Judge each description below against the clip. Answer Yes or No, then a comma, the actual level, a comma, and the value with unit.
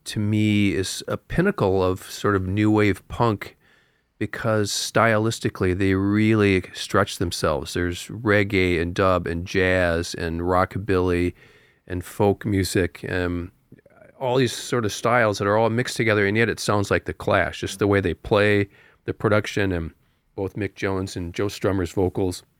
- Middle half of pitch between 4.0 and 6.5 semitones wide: No, narrow, 2.5 semitones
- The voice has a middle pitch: No, low, 100 Hz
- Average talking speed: Yes, average, 160 wpm